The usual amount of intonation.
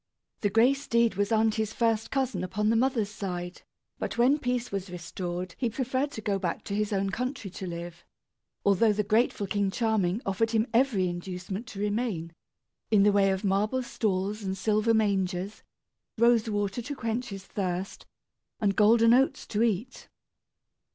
Yes: average, 3.1 semitones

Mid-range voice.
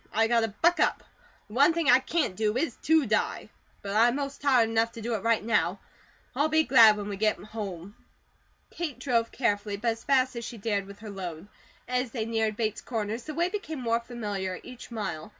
No: high, 230 Hz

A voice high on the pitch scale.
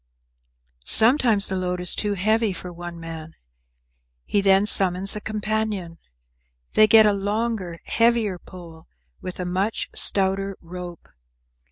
Yes: high, 195 Hz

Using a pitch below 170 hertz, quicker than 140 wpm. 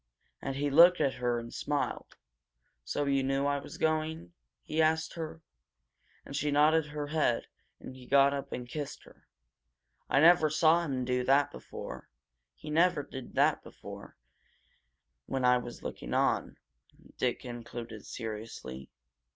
Yes: medium, 140 Hz; average, 150 wpm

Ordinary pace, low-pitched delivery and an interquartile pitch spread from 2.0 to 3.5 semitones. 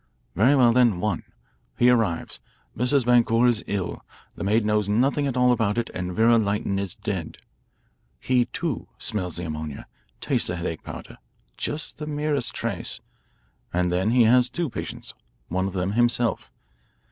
No: average, 160 wpm; low, 115 Hz; average, 4.5 semitones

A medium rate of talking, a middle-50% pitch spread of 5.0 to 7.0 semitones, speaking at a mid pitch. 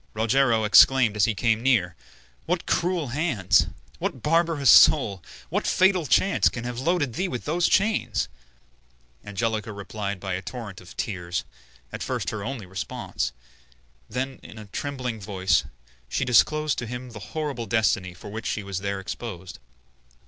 No: average, 155 wpm; wide, 5.4 semitones; low, 115 Hz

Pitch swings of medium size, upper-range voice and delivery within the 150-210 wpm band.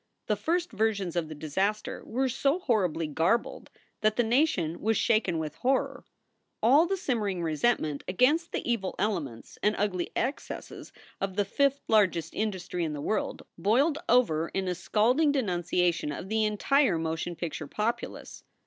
No: wide, 6.0 semitones; high, 210 Hz; average, 155 wpm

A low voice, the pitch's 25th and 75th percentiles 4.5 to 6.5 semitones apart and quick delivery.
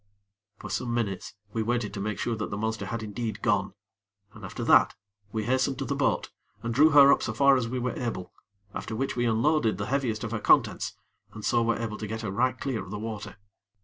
No: low, 115 Hz; average, 2.9 semitones; fast, 230 wpm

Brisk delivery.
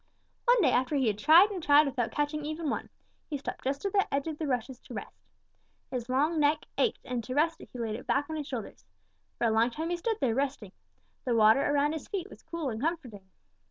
Yes: fast, 240 wpm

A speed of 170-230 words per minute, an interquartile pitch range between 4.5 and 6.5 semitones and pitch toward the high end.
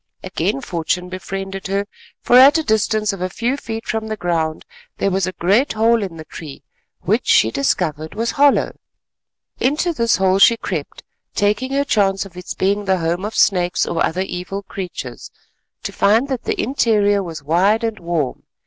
No: average, 180 wpm; average, 4.0 semitones; high, 195 Hz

